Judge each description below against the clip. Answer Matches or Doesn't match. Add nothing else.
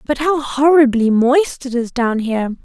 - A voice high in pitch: Matches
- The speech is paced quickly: Doesn't match